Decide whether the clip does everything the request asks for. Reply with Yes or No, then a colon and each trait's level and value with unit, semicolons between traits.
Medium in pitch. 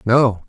No: low, 115 Hz